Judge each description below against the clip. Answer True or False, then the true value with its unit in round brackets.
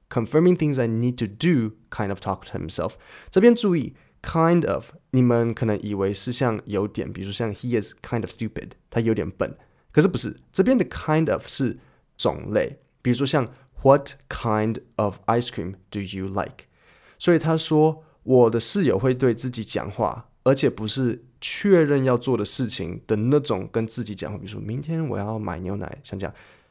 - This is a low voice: True (115 Hz)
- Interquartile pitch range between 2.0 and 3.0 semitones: False (4.3 semitones)